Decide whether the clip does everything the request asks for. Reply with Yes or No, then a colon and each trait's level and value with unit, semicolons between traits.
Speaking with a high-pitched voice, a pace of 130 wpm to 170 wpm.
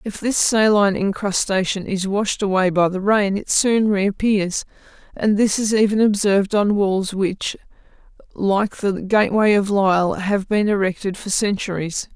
Yes: high, 200 Hz; average, 160 wpm